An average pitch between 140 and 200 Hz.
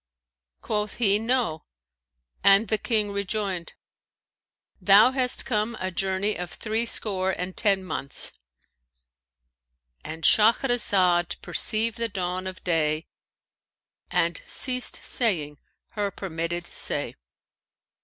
Yes: high, 190 Hz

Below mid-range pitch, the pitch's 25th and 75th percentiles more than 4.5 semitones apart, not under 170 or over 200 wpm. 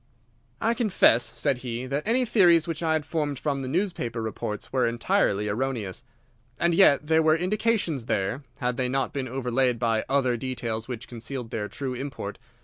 Yes: low, 130 Hz; average, 5.2 semitones; average, 175 wpm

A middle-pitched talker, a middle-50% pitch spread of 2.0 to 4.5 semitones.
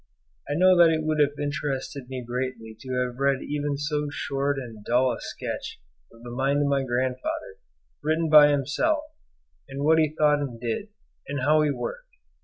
Yes: medium, 145 Hz; average, 2.9 semitones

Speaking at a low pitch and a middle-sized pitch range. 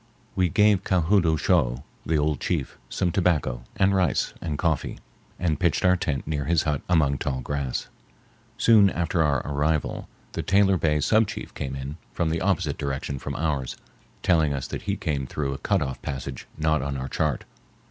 Yes: very low, 80 Hz; average, 4.2 semitones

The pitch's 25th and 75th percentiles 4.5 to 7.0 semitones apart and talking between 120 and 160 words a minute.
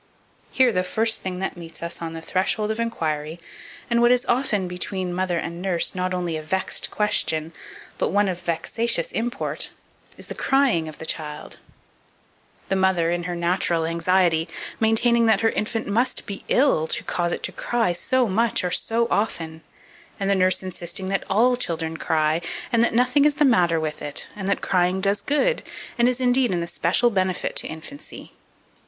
No: average, 5.2 semitones; average, 185 wpm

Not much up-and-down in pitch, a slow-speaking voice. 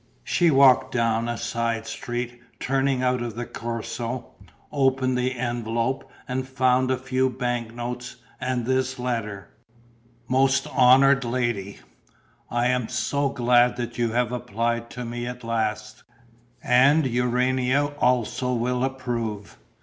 Yes: narrow, 1.7 semitones; slow, 130 wpm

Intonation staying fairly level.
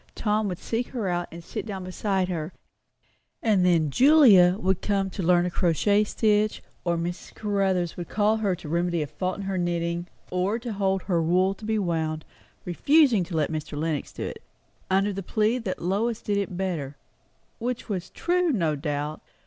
No: average, 3.5 semitones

